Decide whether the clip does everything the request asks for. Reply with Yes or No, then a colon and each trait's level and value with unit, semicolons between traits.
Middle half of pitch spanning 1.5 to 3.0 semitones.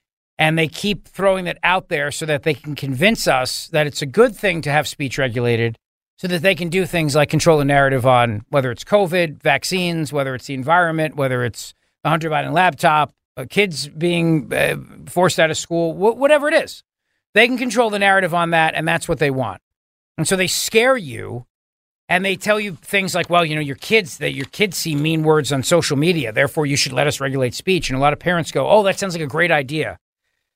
No: average, 4.5 semitones